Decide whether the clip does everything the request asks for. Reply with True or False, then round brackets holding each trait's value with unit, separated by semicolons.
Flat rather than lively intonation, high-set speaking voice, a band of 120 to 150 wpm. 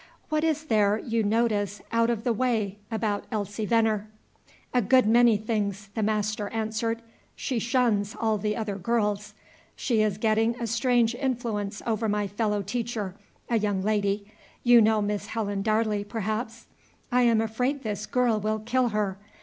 False (2.1 semitones; 220 Hz; 160 wpm)